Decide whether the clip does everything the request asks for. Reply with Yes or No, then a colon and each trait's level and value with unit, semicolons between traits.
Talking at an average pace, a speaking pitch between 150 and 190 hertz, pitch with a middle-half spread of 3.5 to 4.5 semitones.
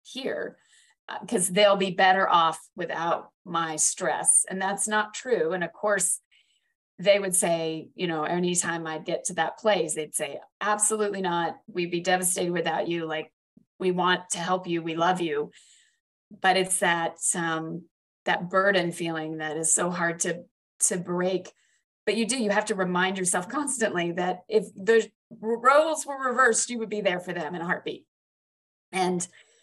Yes: average, 170 wpm; medium, 185 Hz; average, 3.8 semitones